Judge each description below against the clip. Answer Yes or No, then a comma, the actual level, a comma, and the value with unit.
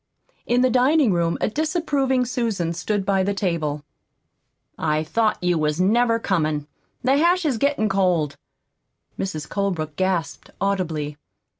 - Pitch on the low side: No, high, 195 Hz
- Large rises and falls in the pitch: Yes, wide, 7.1 semitones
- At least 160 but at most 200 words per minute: No, slow, 135 wpm